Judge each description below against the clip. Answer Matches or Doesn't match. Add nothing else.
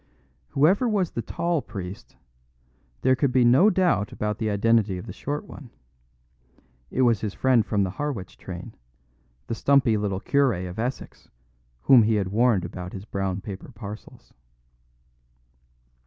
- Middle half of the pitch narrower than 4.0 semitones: Doesn't match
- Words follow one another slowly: Doesn't match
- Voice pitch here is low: Matches